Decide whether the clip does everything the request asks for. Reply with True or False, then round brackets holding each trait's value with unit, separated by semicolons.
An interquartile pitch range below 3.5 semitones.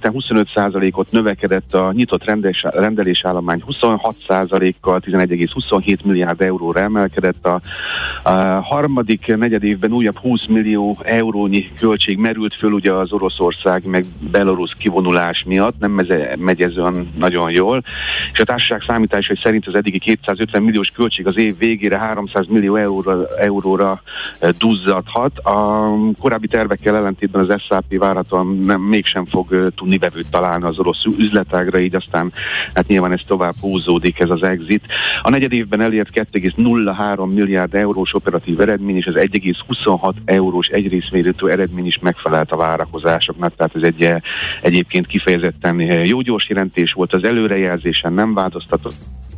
True (2.8 semitones)